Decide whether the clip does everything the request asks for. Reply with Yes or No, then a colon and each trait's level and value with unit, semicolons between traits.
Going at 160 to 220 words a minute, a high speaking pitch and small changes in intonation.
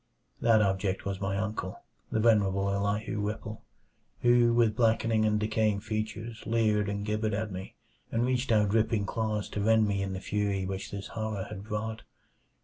No: average, 170 wpm; low, 105 Hz; narrow, 1.8 semitones